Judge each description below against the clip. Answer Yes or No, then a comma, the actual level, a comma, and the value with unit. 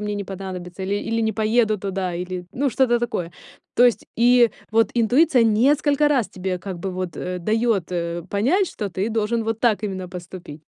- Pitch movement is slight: No, average, 4.3 semitones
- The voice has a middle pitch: No, high, 210 Hz